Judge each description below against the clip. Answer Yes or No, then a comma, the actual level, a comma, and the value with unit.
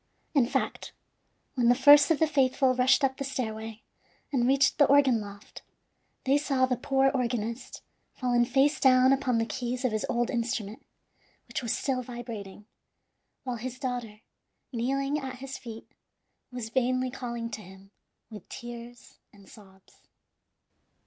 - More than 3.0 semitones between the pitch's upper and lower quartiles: No, narrow, 2.6 semitones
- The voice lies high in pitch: Yes, very high, 250 Hz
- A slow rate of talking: No, average, 150 wpm